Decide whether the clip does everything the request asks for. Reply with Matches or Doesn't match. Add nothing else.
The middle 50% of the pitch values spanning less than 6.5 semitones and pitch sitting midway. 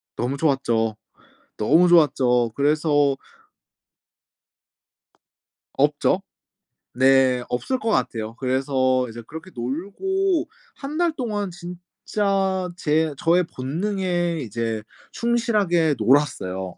Doesn't match